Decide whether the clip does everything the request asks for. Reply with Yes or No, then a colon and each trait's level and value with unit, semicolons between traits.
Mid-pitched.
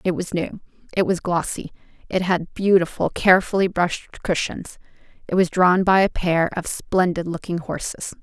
Yes: medium, 180 Hz